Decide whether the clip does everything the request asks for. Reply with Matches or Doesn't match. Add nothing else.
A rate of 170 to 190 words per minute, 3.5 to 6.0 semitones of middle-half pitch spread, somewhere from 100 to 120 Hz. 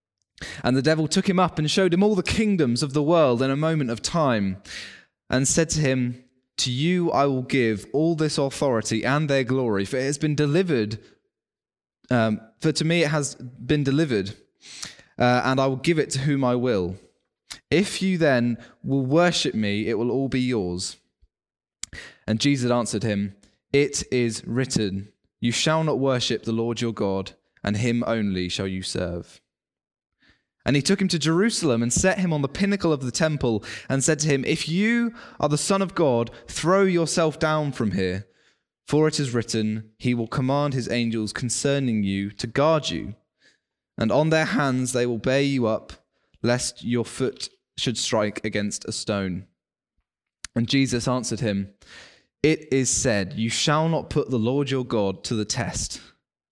Doesn't match